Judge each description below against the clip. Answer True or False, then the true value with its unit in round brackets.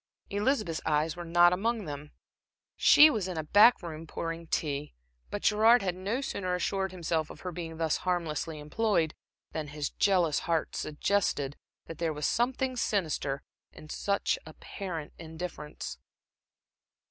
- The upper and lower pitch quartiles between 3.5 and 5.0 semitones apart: True (4.3 semitones)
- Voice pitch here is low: False (170 Hz)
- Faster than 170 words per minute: False (145 wpm)